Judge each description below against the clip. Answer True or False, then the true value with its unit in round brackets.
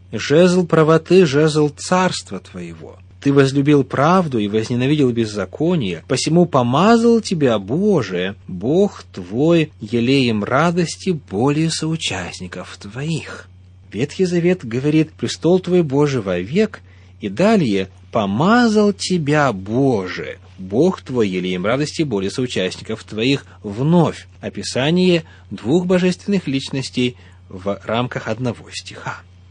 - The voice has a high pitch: False (130 Hz)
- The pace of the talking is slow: True (100 wpm)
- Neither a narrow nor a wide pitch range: False (8.9 semitones)